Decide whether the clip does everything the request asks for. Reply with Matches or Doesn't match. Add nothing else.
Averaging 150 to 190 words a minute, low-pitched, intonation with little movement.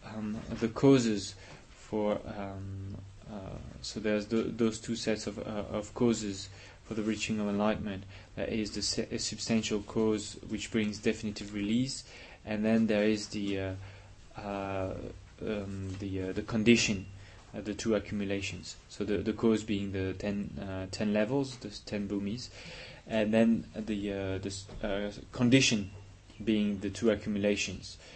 Matches